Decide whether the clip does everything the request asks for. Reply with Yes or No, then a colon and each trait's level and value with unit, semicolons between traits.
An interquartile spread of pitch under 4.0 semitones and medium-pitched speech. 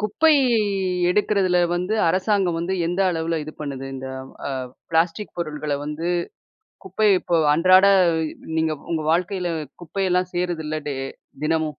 Yes: average, 2.8 semitones; medium, 175 Hz